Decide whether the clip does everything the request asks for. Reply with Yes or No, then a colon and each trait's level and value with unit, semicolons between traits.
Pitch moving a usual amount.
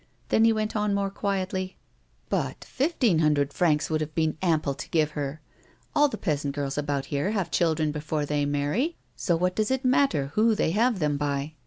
No: wide, 6.0 semitones